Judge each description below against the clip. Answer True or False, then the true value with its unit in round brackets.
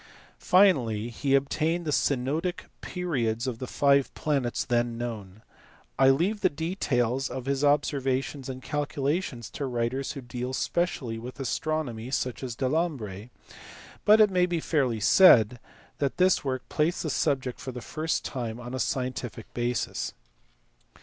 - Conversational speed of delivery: True (145 wpm)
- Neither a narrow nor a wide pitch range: True (4.0 semitones)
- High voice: False (135 Hz)